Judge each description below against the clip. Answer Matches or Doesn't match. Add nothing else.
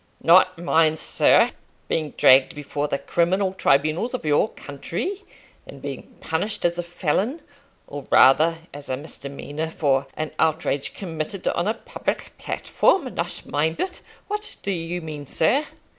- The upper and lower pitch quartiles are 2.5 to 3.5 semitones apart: Doesn't match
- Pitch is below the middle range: Doesn't match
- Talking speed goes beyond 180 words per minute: Doesn't match